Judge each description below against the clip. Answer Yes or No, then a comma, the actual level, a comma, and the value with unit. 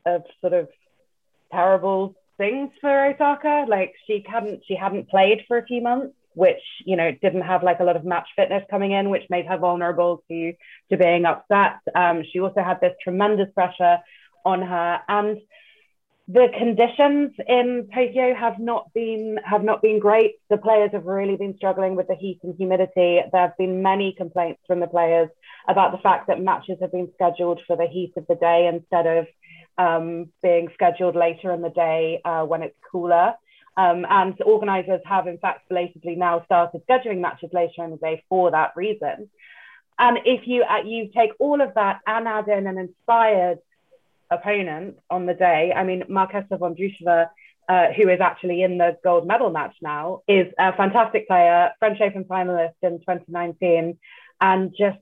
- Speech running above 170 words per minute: Yes, average, 185 wpm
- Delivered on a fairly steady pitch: No, average, 3.4 semitones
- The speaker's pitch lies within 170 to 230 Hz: Yes, medium, 185 Hz